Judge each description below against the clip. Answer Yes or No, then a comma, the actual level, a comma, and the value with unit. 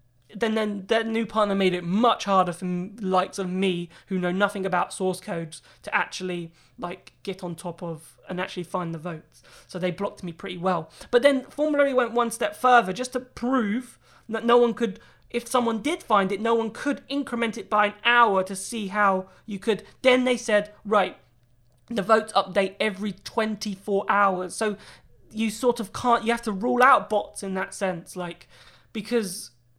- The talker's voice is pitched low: No, high, 205 Hz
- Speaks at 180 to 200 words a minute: Yes, average, 195 wpm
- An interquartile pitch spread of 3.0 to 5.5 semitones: Yes, average, 4.0 semitones